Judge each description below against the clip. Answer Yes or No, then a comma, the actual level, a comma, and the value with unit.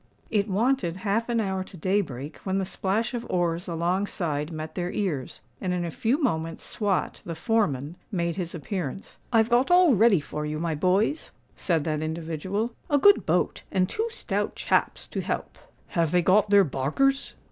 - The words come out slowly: No, average, 180 wpm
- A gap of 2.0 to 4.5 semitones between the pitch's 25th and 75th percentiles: No, average, 5.2 semitones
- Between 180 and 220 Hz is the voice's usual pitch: Yes, medium, 185 Hz